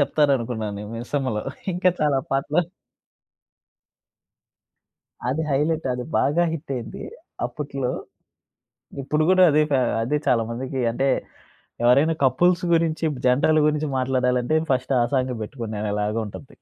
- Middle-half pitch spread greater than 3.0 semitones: Yes, average, 3.7 semitones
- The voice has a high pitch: No, low, 135 Hz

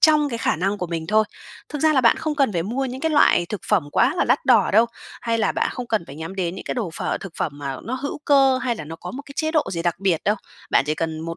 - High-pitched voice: Yes, high, 220 Hz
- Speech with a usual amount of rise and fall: No, wide, 7.7 semitones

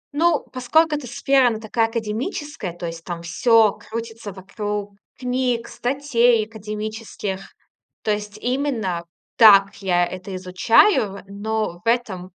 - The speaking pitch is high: Yes, high, 220 Hz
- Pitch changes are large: No, average, 3.7 semitones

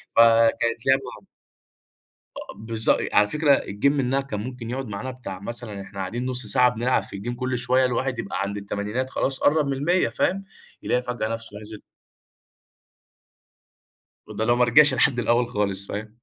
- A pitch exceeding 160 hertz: No, low, 120 Hz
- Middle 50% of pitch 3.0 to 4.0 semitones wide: Yes, average, 3.4 semitones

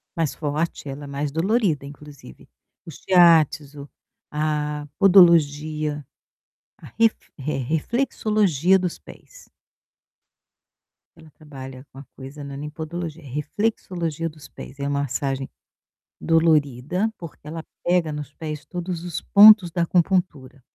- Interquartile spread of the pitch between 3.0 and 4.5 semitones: Yes, average, 3.4 semitones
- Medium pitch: Yes, medium, 155 Hz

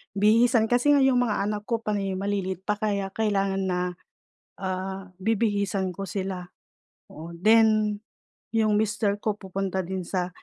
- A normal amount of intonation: No, narrow, 2.1 semitones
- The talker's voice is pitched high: Yes, high, 200 Hz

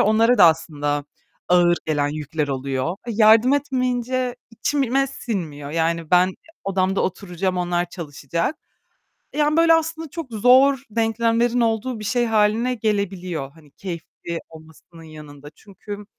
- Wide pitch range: Yes, wide, 7.0 semitones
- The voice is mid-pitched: No, high, 195 Hz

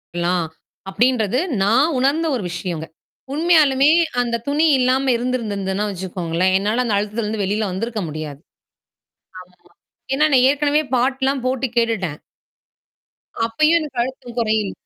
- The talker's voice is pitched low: No, high, 235 Hz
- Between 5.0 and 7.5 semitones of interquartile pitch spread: Yes, wide, 5.6 semitones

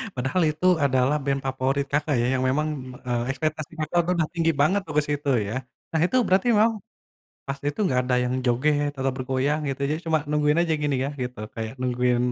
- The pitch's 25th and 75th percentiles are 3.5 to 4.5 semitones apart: No, average, 3.1 semitones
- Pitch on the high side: No, medium, 145 Hz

